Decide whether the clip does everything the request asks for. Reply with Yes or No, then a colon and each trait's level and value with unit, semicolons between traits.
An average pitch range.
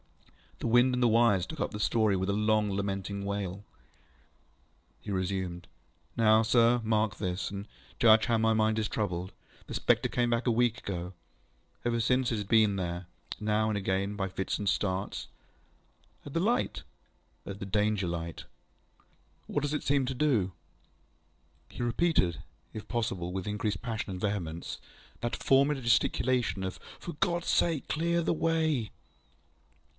Yes: average, 3.9 semitones